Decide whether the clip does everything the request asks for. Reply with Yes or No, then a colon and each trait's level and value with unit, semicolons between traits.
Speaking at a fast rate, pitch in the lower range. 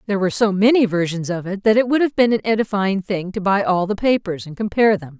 No: fast, 265 wpm; high, 200 Hz